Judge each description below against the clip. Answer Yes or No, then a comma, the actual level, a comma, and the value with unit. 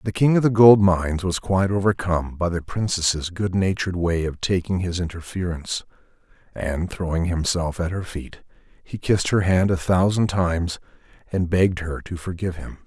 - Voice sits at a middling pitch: No, very low, 90 Hz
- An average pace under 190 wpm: Yes, average, 175 wpm